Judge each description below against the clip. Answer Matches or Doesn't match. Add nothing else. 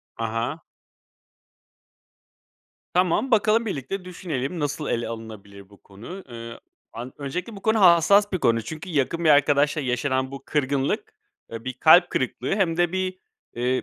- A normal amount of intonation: Doesn't match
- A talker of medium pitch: Matches